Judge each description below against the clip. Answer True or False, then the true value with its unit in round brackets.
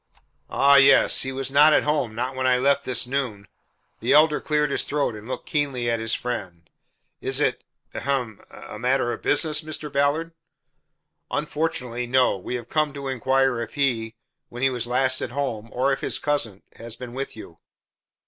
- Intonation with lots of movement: False (3.0 semitones)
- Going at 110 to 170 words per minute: False (185 wpm)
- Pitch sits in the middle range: False (130 Hz)